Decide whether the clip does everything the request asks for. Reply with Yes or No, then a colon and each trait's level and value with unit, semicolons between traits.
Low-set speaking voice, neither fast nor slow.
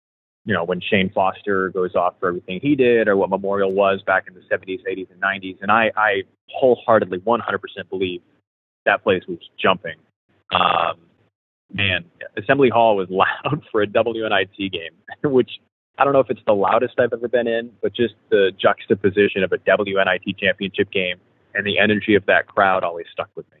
Yes: low, 100 Hz; average, 185 wpm